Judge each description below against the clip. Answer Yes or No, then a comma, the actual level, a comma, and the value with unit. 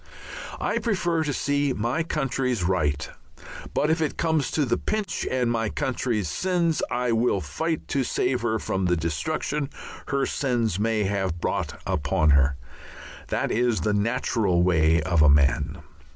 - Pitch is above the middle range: No, low, 115 Hz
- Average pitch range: No, wide, 8.3 semitones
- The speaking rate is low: No, average, 155 wpm